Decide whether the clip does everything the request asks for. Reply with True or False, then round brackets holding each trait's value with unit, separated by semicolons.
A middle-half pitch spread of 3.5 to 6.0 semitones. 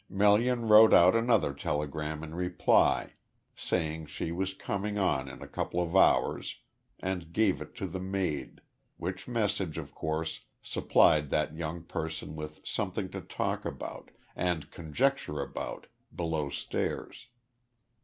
True (4.2 semitones)